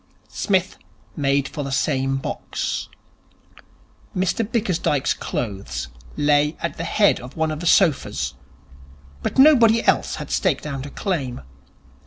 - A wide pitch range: Yes, wide, 5.7 semitones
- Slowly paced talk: Yes, slow, 130 wpm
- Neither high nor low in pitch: Yes, medium, 150 Hz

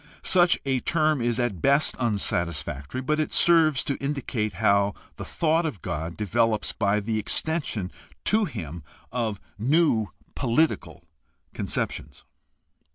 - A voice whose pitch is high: No, low, 120 Hz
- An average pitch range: No, wide, 7.4 semitones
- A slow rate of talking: Yes, slow, 125 wpm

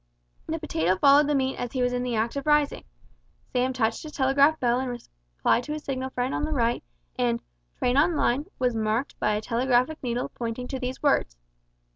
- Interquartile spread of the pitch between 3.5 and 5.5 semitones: No, average, 3.1 semitones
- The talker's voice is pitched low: No, very high, 250 Hz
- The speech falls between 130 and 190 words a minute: No, fast, 205 wpm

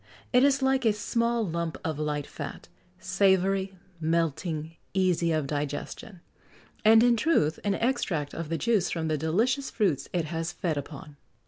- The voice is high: No, medium, 175 Hz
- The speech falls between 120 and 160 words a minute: Yes, average, 155 wpm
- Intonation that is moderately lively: No, wide, 5.8 semitones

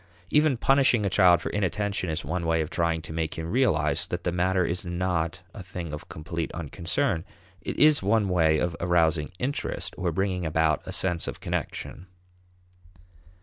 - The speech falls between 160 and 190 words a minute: Yes, average, 175 wpm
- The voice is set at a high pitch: No, very low, 85 Hz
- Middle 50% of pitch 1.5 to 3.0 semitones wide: Yes, average, 2.7 semitones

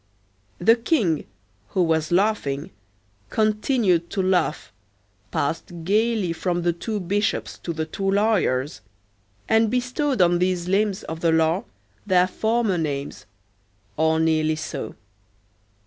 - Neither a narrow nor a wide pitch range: Yes, average, 4.7 semitones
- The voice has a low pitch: No, medium, 180 Hz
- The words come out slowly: Yes, slow, 120 wpm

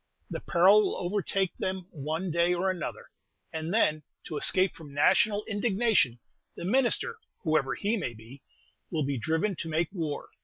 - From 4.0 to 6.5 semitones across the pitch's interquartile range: Yes, average, 4.5 semitones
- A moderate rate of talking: Yes, average, 160 wpm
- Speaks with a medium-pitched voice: Yes, medium, 175 Hz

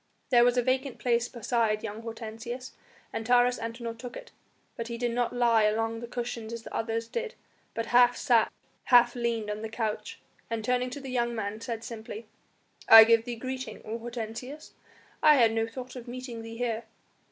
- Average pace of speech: Yes, average, 190 wpm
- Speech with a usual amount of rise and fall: No, narrow, 1.5 semitones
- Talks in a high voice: Yes, high, 235 Hz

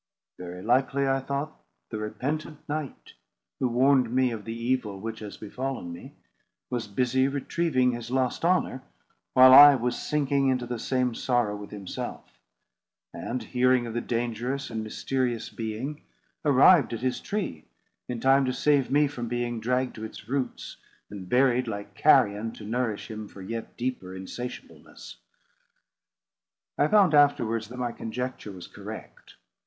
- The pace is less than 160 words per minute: Yes, average, 150 wpm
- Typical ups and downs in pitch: Yes, average, 3.1 semitones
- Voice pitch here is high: No, low, 125 Hz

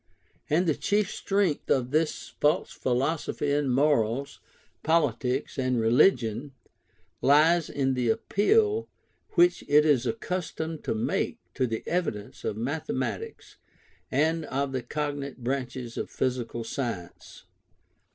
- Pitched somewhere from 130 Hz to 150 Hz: Yes, medium, 140 Hz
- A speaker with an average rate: No, slow, 120 wpm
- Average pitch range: Yes, average, 4.3 semitones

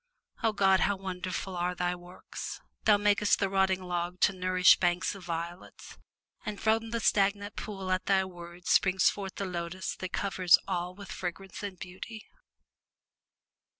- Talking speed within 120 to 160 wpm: Yes, average, 155 wpm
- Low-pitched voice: No, medium, 185 Hz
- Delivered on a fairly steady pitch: Yes, narrow, 1.9 semitones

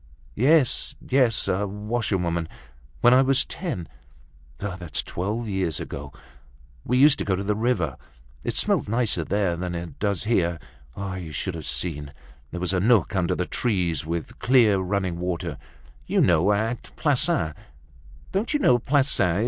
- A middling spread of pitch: No, wide, 6.3 semitones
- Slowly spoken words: Yes, slow, 130 wpm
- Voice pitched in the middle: No, very low, 95 Hz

